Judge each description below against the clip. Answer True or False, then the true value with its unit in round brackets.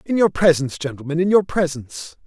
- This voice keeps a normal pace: True (185 wpm)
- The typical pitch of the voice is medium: True (165 Hz)